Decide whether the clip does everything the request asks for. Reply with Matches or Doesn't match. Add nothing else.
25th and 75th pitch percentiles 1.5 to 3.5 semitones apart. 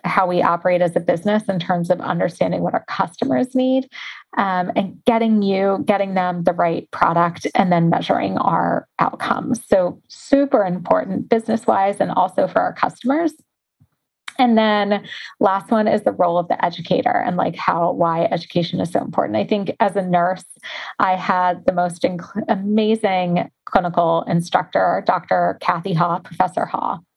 Doesn't match